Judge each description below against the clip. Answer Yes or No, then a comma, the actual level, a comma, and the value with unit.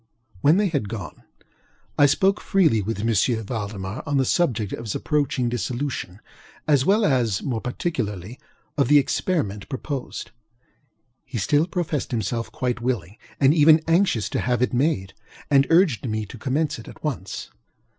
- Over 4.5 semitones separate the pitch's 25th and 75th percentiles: Yes, wide, 5.4 semitones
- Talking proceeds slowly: No, average, 155 wpm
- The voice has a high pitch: No, low, 125 Hz